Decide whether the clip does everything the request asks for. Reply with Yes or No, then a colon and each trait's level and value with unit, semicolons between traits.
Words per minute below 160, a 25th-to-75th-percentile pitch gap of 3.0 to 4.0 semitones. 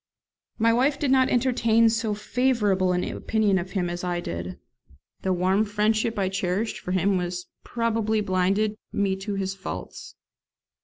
Yes: average, 150 wpm; average, 3.3 semitones